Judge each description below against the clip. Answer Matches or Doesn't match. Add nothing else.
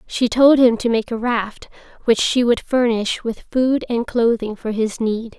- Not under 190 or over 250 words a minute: Matches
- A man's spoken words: Doesn't match